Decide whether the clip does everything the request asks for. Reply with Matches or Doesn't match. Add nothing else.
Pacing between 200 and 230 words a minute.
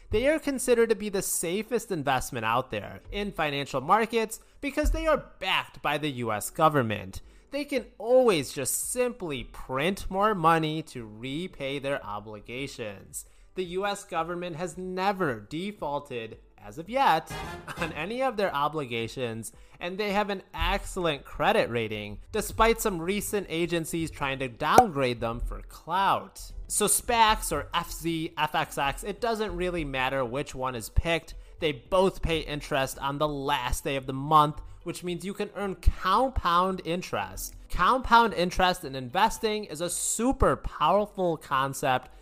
Doesn't match